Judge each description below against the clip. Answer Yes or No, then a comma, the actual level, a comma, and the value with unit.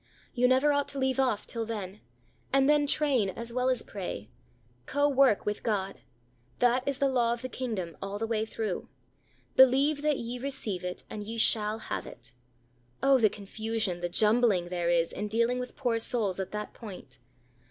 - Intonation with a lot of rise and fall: No, average, 4.2 semitones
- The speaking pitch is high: Yes, high, 230 Hz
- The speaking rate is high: No, average, 185 wpm